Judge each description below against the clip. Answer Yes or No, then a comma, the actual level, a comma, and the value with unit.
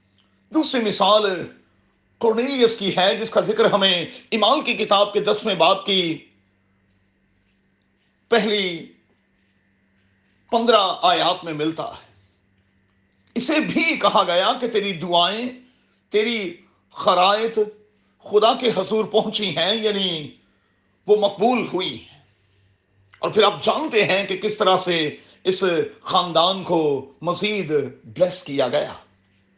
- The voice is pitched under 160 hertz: No, medium, 185 Hz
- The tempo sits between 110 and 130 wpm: Yes, average, 115 wpm